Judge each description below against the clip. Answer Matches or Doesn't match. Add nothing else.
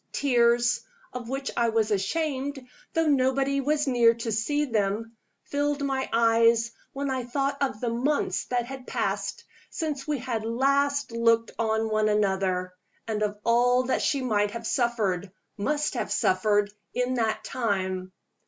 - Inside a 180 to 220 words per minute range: Doesn't match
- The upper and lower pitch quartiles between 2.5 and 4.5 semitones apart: Matches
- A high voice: Matches